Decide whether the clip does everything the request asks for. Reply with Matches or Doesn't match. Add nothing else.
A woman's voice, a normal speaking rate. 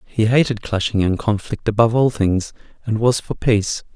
Doesn't match